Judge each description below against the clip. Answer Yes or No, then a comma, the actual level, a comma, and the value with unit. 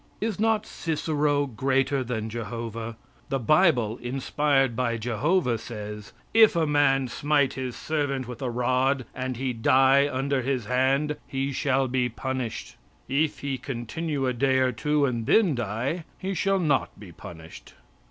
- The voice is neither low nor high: No, low, 130 Hz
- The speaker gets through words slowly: No, average, 150 wpm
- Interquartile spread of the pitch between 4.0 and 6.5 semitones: No, average, 3.3 semitones